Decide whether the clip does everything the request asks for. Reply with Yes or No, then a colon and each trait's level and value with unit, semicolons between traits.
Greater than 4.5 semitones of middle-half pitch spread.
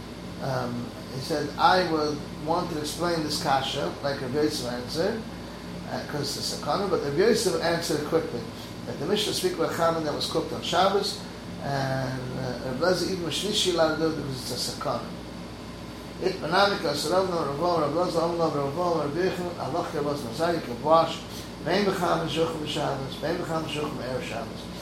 Yes: average, 5.1 semitones